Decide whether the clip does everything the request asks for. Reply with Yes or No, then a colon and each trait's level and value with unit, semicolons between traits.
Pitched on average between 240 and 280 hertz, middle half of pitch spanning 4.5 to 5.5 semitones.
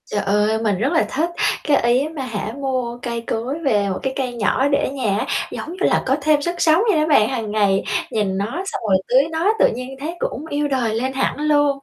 Yes: very high, 260 Hz; average, 5.1 semitones